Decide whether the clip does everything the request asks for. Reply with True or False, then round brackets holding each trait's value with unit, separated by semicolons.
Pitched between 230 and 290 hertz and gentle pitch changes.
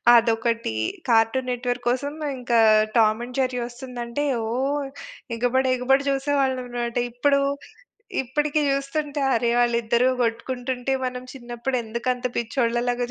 True (250 Hz; 2.2 semitones)